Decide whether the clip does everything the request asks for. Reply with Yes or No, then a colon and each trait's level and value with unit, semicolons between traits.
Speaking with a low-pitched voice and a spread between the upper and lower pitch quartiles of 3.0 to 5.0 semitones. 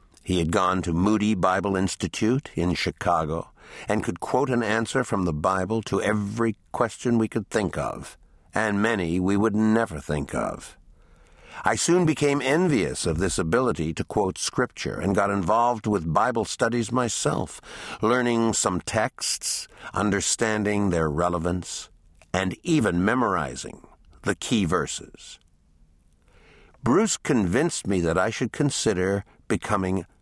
Yes: very low, 95 Hz; average, 4.5 semitones